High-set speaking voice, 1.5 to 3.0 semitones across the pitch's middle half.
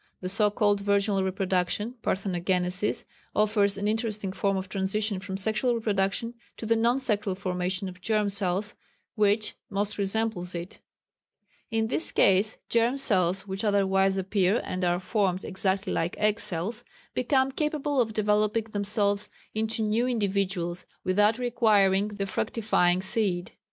Yes: high, 200 Hz; narrow, 2.5 semitones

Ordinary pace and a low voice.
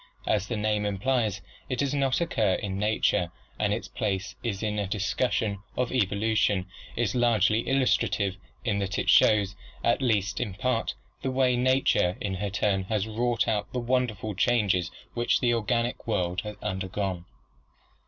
Yes: average, 160 wpm; low, 105 Hz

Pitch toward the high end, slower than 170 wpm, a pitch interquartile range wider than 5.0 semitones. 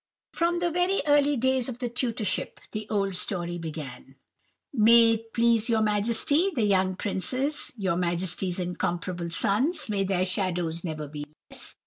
Yes: high, 210 Hz; average, 140 wpm; wide, 5.6 semitones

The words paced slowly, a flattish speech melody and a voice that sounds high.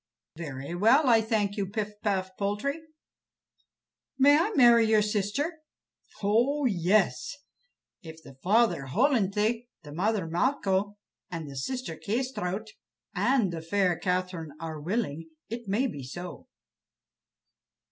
No: slow, 115 wpm; average, 5.2 semitones; high, 205 Hz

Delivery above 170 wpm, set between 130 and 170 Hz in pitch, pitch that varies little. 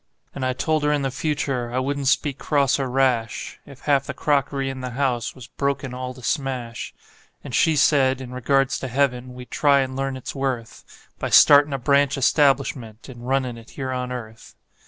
Yes: average, 200 wpm; low, 135 Hz; narrow, 1.8 semitones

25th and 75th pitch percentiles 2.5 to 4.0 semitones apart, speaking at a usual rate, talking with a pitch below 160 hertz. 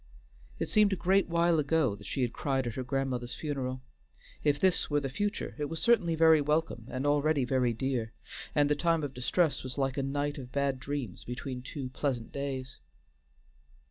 Yes: average, 3.4 semitones; average, 190 wpm; medium, 140 Hz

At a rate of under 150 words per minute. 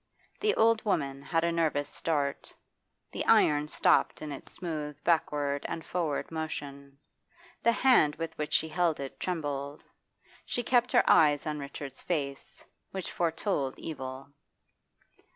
Yes: slow, 135 wpm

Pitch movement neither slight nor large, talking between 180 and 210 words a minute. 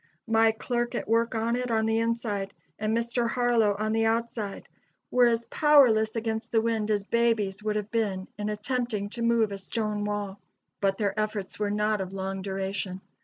No: narrow, 2.2 semitones; average, 185 wpm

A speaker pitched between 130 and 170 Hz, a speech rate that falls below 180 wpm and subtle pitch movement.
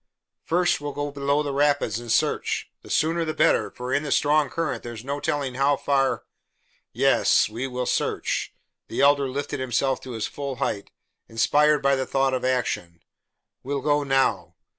No: medium, 140 Hz; average, 185 wpm; narrow, 2.3 semitones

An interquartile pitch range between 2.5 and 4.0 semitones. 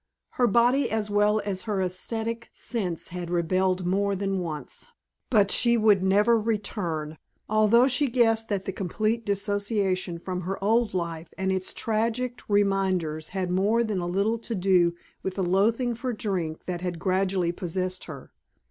Yes: average, 3.4 semitones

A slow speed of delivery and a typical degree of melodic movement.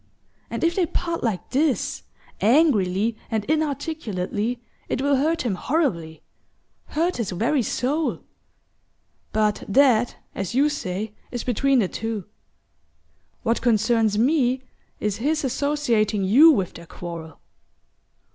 No: slow, 120 wpm; wide, 6.0 semitones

